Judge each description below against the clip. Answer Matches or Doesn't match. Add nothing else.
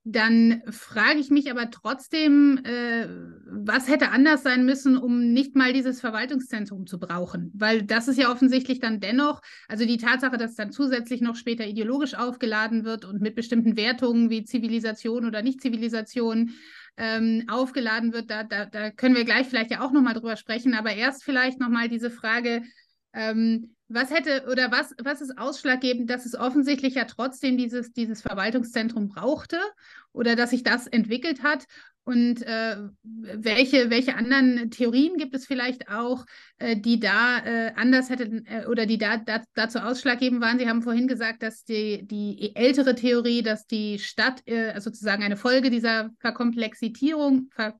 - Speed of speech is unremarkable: Matches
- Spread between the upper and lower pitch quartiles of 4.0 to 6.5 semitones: Doesn't match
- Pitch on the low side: Doesn't match